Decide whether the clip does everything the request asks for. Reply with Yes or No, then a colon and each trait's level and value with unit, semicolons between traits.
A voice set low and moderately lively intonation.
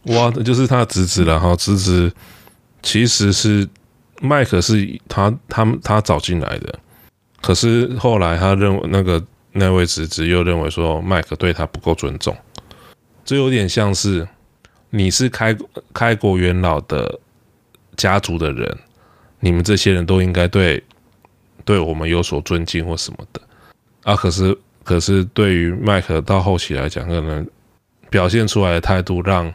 Yes: very low, 95 Hz; average, 3.6 semitones